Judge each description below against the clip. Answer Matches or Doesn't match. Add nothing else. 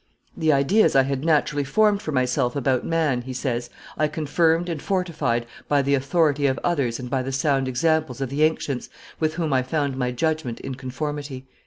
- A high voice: Doesn't match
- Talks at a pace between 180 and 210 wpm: Matches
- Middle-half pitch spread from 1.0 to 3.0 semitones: Doesn't match